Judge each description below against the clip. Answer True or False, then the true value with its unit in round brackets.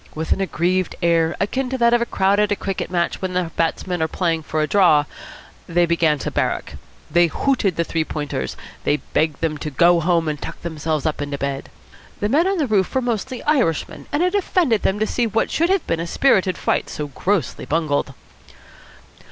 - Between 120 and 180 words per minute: False (205 wpm)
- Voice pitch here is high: False (175 Hz)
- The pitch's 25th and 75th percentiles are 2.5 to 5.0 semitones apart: False (5.4 semitones)